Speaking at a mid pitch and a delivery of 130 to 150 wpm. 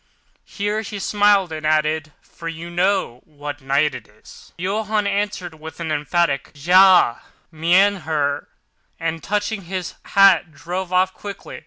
Yes: medium, 175 Hz; average, 140 wpm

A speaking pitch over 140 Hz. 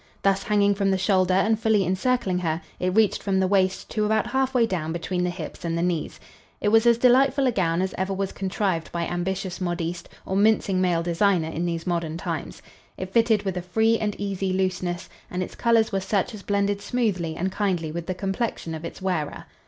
Yes: high, 190 Hz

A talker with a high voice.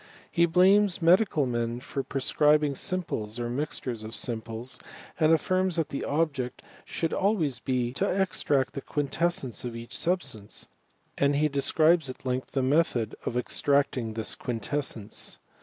No: medium, 140 Hz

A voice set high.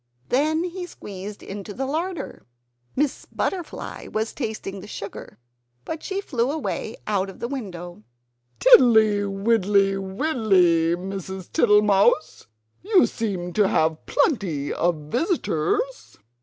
Yes: high, 210 Hz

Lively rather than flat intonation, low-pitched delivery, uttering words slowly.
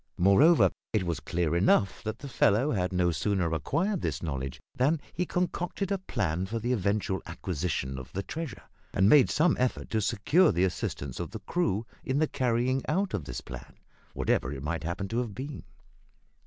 No: wide, 8.1 semitones; low, 100 Hz; average, 185 wpm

